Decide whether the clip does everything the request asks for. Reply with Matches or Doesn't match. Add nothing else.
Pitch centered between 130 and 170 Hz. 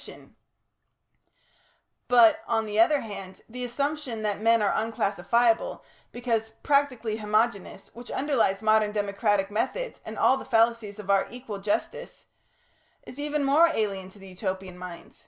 Doesn't match